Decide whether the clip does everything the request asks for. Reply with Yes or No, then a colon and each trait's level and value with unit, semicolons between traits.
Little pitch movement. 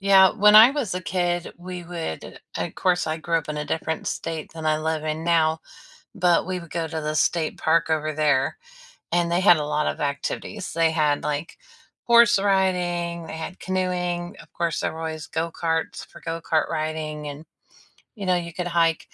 Yes: narrow, 2.2 semitones